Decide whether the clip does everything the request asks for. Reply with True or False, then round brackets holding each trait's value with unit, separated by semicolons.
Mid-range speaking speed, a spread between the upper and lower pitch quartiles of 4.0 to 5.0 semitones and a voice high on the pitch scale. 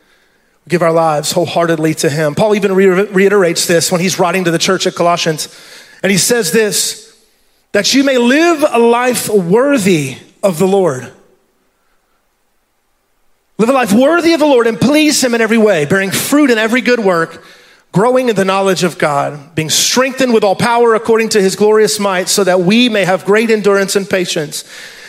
True (180 wpm; 4.5 semitones; 200 Hz)